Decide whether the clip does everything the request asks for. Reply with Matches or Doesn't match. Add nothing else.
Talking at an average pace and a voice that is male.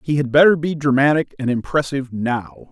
Matches